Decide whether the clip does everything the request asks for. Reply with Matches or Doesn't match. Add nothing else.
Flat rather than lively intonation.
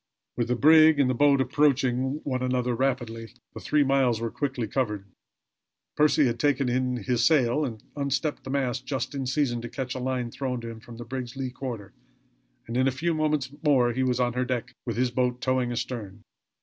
Matches